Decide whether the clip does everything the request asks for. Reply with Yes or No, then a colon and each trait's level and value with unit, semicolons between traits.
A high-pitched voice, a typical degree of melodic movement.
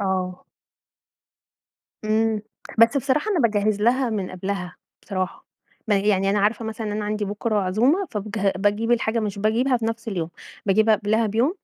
No: high, 215 Hz; narrow, 2.3 semitones